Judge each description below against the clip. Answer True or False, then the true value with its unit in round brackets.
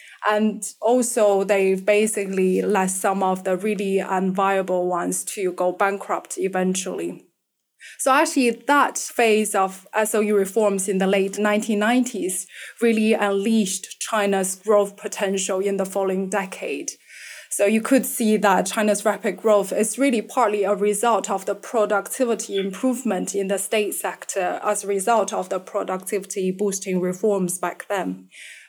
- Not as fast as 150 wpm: True (140 wpm)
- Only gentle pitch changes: True (2.0 semitones)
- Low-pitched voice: False (200 Hz)